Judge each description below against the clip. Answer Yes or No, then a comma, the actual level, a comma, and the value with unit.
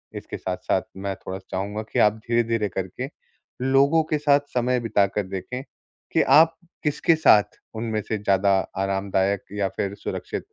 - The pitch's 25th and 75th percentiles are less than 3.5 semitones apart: No, average, 4.5 semitones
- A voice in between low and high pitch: No, low, 105 Hz